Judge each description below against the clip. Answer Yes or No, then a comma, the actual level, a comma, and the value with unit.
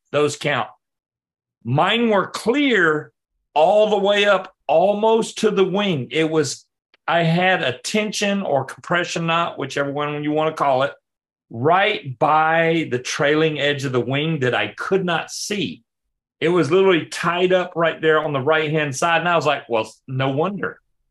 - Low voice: No, medium, 160 Hz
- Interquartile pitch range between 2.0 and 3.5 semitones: No, average, 4.3 semitones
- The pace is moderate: Yes, average, 175 wpm